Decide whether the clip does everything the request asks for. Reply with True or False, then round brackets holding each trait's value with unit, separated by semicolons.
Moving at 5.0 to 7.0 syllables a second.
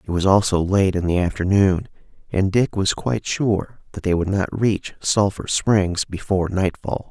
False (4.6 syllables/s)